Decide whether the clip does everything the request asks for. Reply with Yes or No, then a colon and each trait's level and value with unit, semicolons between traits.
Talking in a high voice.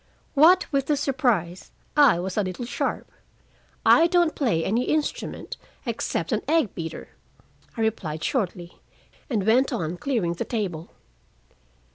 Yes: high, 225 Hz